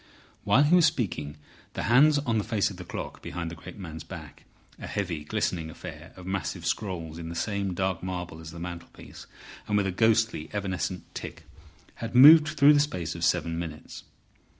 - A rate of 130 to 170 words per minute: No, average, 180 wpm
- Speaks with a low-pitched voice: Yes, very low, 95 Hz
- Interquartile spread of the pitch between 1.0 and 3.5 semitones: No, average, 5.0 semitones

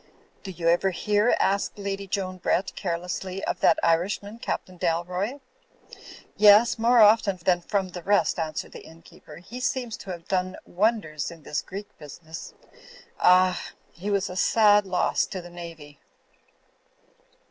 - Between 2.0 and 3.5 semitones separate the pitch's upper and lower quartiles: Yes, average, 3.1 semitones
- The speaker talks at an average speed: Yes, average, 150 wpm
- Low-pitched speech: No, medium, 185 Hz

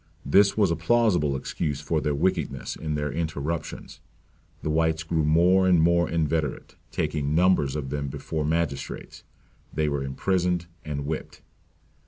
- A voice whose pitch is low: Yes, very low, 80 Hz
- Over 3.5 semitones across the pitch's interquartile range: No, average, 2.8 semitones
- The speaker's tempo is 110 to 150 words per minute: Yes, average, 145 wpm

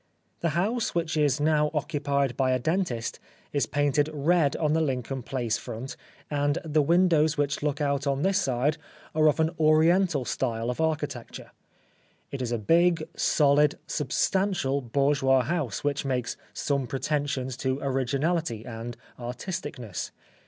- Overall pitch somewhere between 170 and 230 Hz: No, medium, 145 Hz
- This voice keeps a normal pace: Yes, average, 145 wpm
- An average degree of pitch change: Yes, average, 3.2 semitones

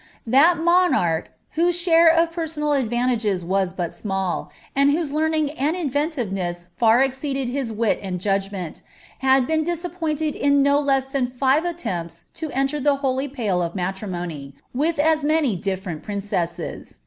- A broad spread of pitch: Yes, wide, 7.9 semitones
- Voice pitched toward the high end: Yes, very high, 270 Hz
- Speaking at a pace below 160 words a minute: Yes, average, 150 wpm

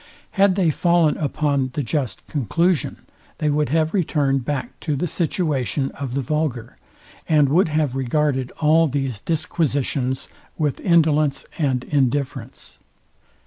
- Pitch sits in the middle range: Yes, medium, 145 Hz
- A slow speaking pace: Yes, slow, 130 wpm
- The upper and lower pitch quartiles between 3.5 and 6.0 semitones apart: No, average, 3.0 semitones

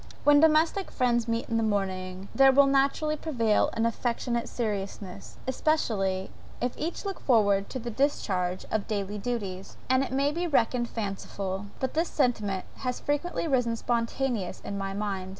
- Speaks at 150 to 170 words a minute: Yes, average, 160 wpm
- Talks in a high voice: Yes, high, 230 Hz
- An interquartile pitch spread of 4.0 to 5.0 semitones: No, wide, 5.4 semitones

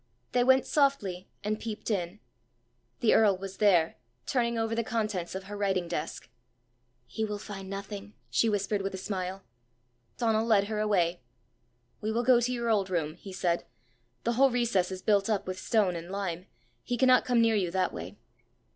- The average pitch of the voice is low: No, high, 205 Hz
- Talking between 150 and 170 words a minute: No, average, 180 wpm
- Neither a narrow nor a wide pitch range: Yes, average, 3.4 semitones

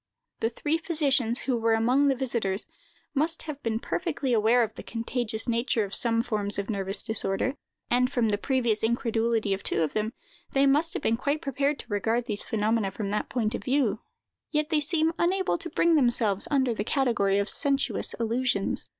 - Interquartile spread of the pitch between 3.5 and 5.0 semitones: Yes, average, 4.2 semitones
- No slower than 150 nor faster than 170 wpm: No, average, 190 wpm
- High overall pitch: Yes, high, 235 Hz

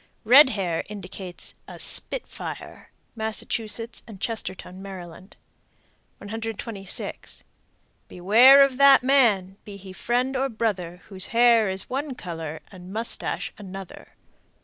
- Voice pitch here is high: Yes, high, 210 Hz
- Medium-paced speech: No, slow, 115 wpm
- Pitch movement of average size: Yes, average, 4.2 semitones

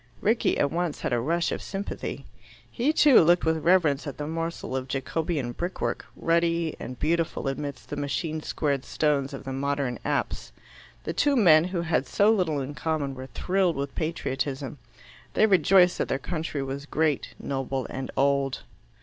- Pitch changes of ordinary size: Yes, average, 3.8 semitones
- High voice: No, medium, 155 Hz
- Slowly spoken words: No, average, 170 wpm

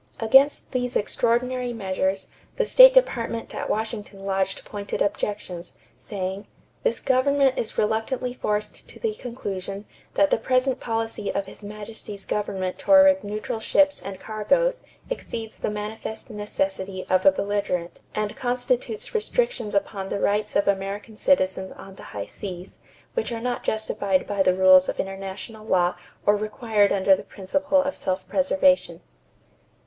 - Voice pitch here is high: Yes, high, 210 Hz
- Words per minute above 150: No, average, 145 wpm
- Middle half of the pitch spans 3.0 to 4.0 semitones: No, average, 4.6 semitones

